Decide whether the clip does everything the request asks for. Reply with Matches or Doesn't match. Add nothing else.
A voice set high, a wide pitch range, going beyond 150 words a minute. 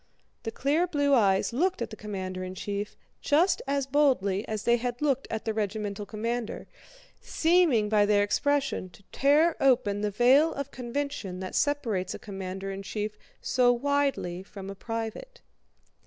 Matches